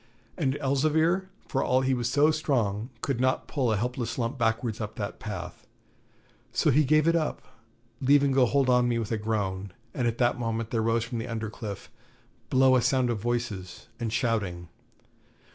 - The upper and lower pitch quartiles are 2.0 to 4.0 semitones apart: Yes, average, 3.1 semitones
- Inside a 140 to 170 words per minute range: No, average, 185 wpm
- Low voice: Yes, low, 120 Hz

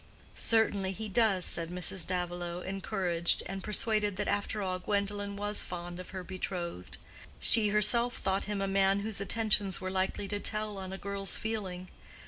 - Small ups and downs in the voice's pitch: Yes, narrow, 2.1 semitones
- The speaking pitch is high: Yes, high, 195 Hz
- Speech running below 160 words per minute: No, average, 165 wpm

